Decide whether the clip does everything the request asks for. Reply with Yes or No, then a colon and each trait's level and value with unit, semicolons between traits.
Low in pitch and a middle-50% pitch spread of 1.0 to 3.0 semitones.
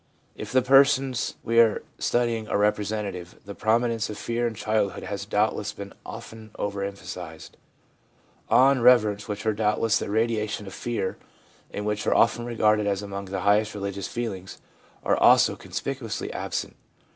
Yes: low, 105 Hz; narrow, 2.5 semitones